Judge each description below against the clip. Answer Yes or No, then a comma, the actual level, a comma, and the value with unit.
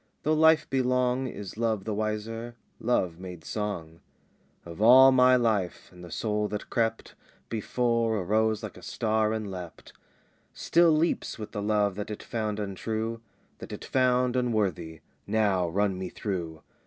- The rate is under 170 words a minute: Yes, average, 155 wpm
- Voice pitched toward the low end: Yes, low, 110 Hz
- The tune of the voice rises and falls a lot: No, average, 3.4 semitones